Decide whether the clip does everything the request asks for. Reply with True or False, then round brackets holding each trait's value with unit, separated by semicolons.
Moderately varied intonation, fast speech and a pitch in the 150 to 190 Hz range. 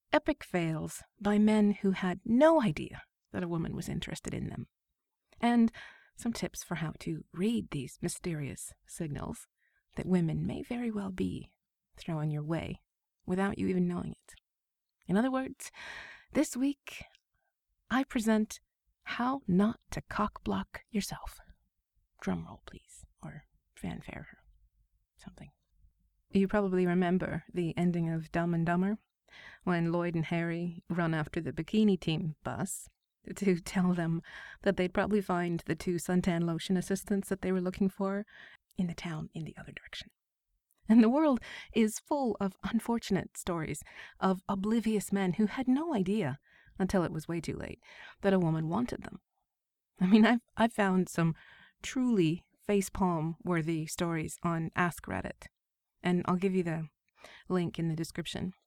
False (4.2 semitones; 150 wpm; 185 Hz)